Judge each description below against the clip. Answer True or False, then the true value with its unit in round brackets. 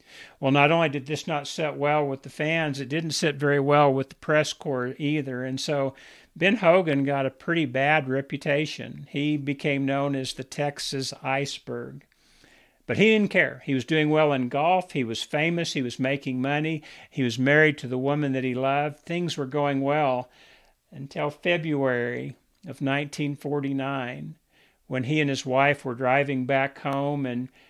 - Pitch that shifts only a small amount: True (2.0 semitones)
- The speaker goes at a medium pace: True (175 wpm)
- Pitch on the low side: False (145 Hz)